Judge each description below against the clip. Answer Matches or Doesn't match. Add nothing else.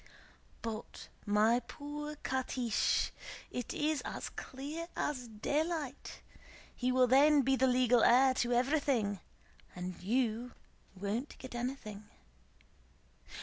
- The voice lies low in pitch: Doesn't match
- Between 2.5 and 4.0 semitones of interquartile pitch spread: Matches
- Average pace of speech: Doesn't match